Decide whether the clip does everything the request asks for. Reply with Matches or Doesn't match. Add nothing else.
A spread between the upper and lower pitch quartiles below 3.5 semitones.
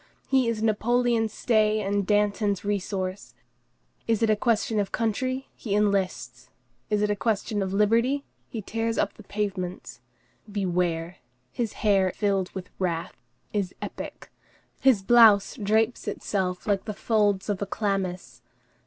Matches